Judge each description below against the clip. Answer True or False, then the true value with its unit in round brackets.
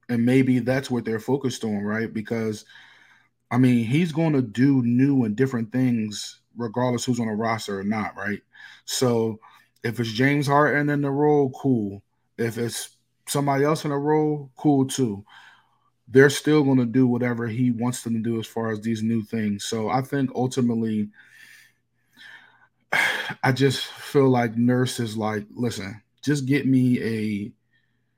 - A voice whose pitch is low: True (120 Hz)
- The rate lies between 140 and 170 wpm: True (165 wpm)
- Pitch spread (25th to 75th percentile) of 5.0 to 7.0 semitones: False (2.8 semitones)